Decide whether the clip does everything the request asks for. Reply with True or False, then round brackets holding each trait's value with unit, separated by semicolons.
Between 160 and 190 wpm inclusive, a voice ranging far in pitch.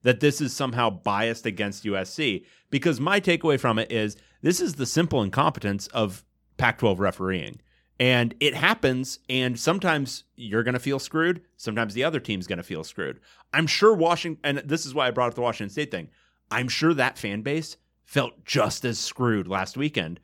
True (185 wpm; 5.9 semitones)